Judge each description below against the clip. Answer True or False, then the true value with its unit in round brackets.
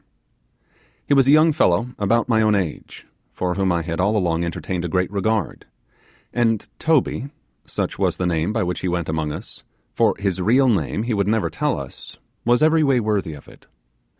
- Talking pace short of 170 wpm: False (195 wpm)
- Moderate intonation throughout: True (5.0 semitones)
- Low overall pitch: True (100 Hz)